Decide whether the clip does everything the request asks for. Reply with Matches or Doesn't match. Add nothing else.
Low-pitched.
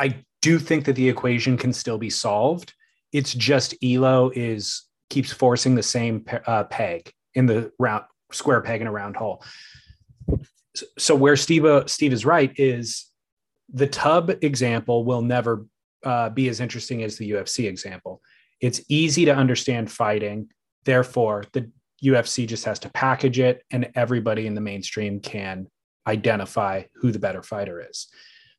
Matches